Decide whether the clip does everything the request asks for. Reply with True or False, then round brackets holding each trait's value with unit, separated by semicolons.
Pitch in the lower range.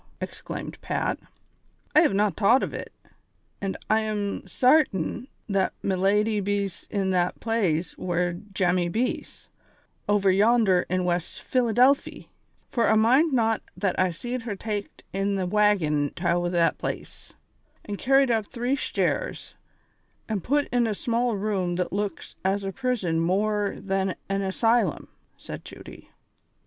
False (205 Hz)